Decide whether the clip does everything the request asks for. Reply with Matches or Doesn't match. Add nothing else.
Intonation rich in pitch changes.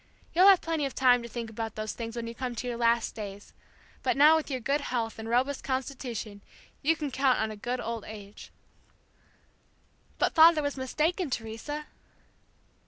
Doesn't match